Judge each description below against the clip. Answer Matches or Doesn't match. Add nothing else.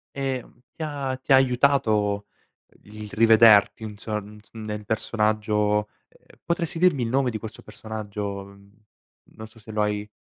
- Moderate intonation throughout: Matches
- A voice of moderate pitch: Doesn't match